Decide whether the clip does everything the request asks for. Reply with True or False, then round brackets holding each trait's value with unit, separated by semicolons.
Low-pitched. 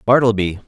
True (110 Hz)